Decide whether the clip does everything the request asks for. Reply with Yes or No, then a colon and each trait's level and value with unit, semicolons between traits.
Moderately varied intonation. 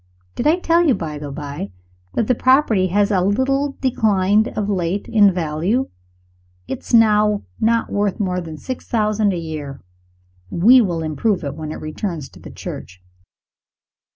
No: wide, 5.8 semitones